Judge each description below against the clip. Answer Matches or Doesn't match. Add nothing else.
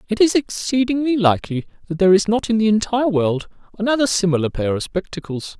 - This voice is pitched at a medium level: Doesn't match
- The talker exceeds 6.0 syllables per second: Matches